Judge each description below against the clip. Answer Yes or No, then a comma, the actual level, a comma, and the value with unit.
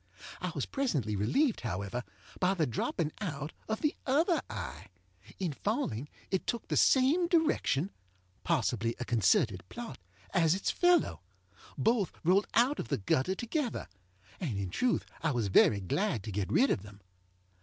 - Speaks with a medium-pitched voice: Yes, medium, 165 Hz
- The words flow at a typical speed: Yes, average, 155 wpm